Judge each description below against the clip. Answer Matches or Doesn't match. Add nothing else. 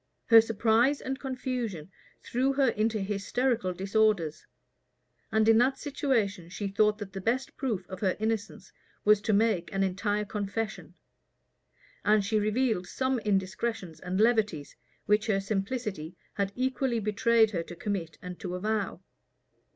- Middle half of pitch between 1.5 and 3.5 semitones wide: Matches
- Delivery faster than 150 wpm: Doesn't match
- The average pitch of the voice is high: Matches